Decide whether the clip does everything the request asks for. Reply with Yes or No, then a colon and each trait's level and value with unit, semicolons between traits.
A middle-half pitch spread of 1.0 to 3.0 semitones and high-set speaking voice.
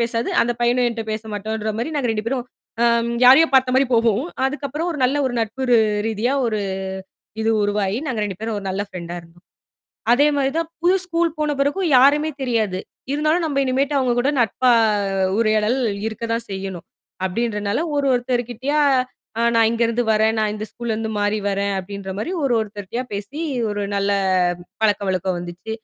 No: average, 4.1 semitones; high, 230 Hz